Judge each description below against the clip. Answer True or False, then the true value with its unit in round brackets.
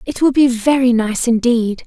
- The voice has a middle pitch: False (240 Hz)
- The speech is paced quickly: False (195 wpm)